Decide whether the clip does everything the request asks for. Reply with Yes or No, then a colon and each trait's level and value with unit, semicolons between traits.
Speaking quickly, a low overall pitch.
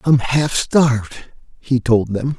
No: average, 150 wpm; low, 125 Hz